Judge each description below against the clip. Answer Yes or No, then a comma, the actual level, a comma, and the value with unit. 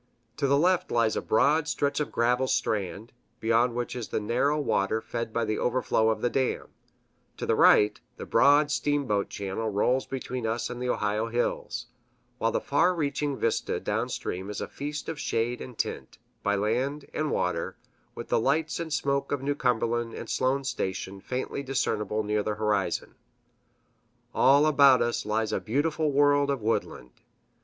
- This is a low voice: Yes, low, 125 Hz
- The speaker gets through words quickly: No, average, 170 wpm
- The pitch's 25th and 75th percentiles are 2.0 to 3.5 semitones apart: No, average, 4.4 semitones